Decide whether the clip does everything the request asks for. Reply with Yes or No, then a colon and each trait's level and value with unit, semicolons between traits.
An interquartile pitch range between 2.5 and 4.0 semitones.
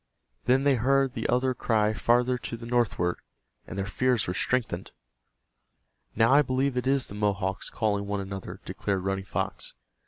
No: average, 4.5 semitones